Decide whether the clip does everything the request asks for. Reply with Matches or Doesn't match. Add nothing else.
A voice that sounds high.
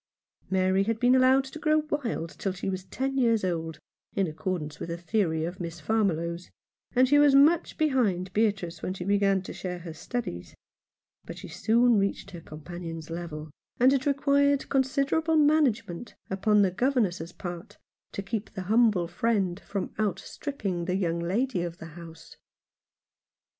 Matches